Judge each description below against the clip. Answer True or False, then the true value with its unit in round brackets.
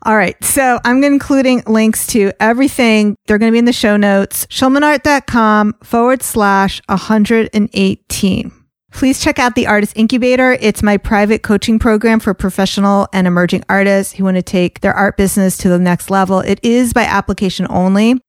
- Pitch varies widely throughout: False (3.5 semitones)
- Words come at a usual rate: True (170 wpm)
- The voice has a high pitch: True (210 Hz)